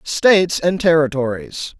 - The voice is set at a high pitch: No, medium, 160 Hz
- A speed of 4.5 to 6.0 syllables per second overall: No, 4.2 syllables/s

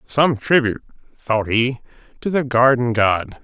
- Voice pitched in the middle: No, low, 125 Hz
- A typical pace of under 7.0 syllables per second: Yes, 4.2 syllables/s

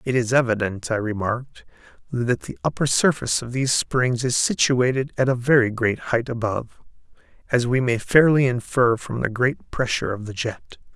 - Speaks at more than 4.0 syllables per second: Yes, 5.2 syllables/s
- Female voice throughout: No, male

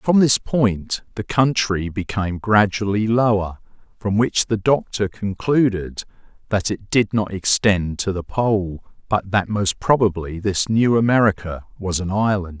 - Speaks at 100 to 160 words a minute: Yes, average, 150 wpm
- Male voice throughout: Yes, male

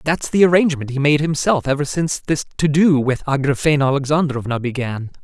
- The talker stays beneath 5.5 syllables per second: No, 6.0 syllables/s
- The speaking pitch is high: No, medium, 145 Hz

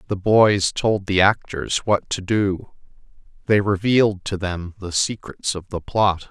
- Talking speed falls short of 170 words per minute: Yes, average, 160 wpm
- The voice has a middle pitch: No, low, 100 Hz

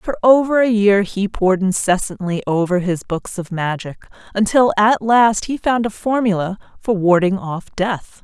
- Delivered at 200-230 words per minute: No, average, 170 wpm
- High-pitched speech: Yes, high, 200 Hz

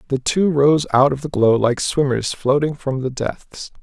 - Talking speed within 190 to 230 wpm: Yes, fast, 205 wpm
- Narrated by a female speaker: No, male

